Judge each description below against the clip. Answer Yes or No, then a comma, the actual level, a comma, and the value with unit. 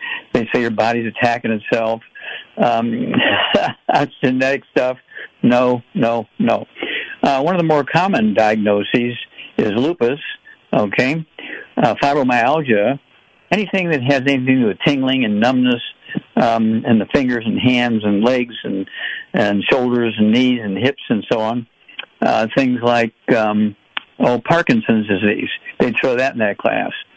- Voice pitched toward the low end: Yes, low, 120 Hz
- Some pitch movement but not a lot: Yes, average, 3.5 semitones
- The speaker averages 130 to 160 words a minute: Yes, average, 145 wpm